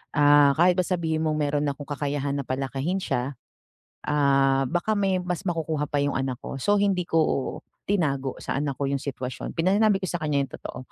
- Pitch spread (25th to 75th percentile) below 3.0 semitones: No, average, 4.0 semitones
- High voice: No, medium, 145 Hz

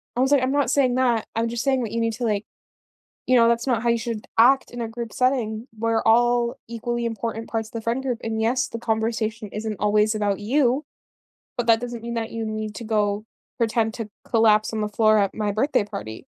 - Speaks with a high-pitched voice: Yes, high, 230 Hz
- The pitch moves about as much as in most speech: No, narrow, 1.8 semitones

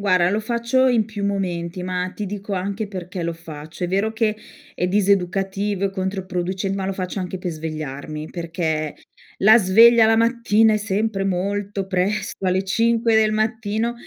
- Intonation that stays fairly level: No, average, 3.0 semitones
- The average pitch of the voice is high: Yes, high, 195 Hz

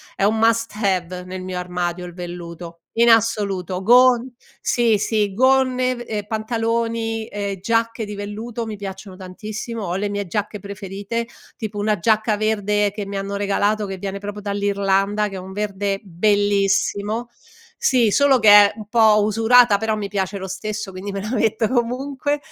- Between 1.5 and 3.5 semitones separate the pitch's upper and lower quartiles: Yes, narrow, 2.4 semitones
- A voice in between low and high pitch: No, high, 205 Hz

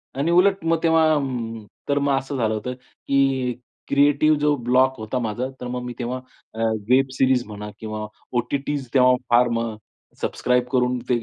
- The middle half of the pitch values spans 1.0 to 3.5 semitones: Yes, narrow, 2.6 semitones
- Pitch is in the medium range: No, low, 125 Hz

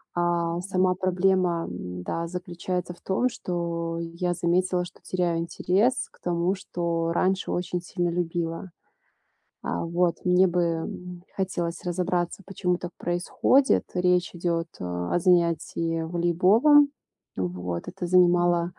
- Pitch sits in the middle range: Yes, medium, 175 Hz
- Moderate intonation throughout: No, narrow, 1.4 semitones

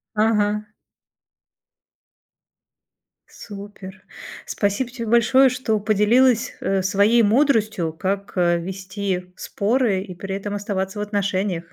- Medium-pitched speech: No, high, 205 Hz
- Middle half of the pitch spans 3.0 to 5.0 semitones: No, narrow, 2.6 semitones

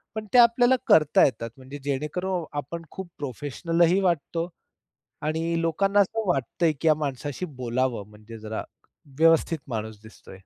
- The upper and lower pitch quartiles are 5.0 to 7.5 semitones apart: Yes, average, 5.3 semitones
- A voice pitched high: No, medium, 155 Hz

